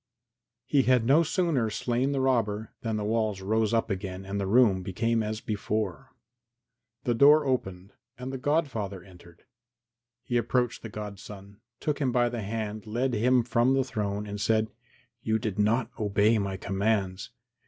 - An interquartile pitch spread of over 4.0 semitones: No, average, 3.5 semitones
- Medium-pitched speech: No, low, 110 Hz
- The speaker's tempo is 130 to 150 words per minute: No, average, 165 wpm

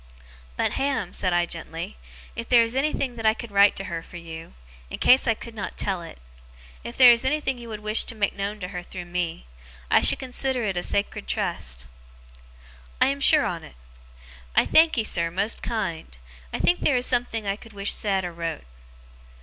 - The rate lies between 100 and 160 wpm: No, average, 200 wpm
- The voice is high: Yes, high, 205 Hz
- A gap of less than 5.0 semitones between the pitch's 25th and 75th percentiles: No, wide, 5.6 semitones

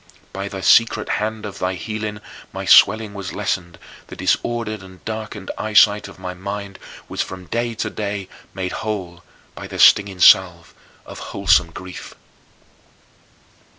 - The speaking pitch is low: Yes, low, 100 Hz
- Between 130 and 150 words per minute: Yes, average, 145 wpm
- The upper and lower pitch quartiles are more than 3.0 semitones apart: No, narrow, 2.6 semitones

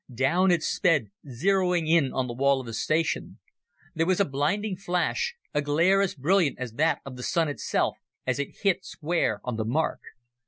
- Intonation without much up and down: No, average, 5.3 semitones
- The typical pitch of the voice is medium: Yes, medium, 155 Hz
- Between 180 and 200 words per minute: Yes, average, 190 wpm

